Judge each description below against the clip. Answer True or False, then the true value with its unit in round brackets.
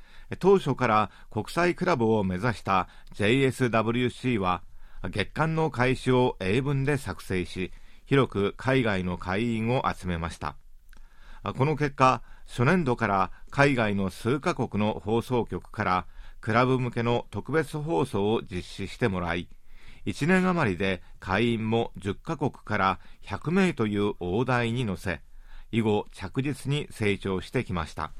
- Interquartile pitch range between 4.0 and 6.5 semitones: True (5.4 semitones)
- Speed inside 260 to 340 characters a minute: False (245 characters per minute)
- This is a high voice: False (110 Hz)